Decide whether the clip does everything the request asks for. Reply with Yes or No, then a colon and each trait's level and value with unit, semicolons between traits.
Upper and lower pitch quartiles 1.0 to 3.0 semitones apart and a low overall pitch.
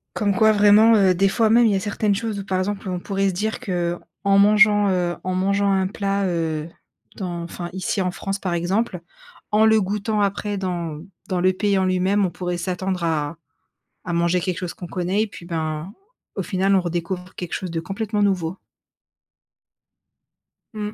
No: narrow, 2.6 semitones; high, 190 Hz